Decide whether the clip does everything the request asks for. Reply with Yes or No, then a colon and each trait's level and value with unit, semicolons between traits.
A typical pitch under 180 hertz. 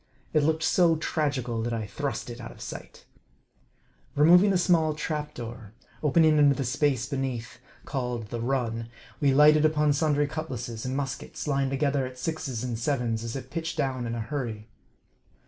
Yes: low, 135 Hz